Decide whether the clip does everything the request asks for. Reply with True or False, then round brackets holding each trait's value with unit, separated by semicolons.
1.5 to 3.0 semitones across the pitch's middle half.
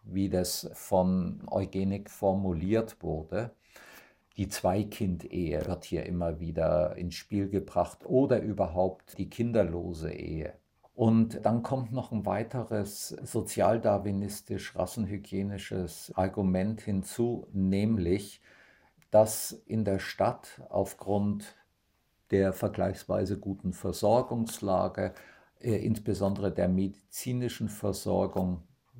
True (2.7 semitones)